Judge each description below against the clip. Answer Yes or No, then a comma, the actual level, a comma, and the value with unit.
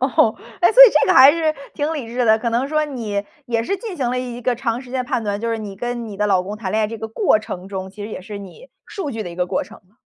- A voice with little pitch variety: No, average, 4.1 semitones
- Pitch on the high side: Yes, high, 230 Hz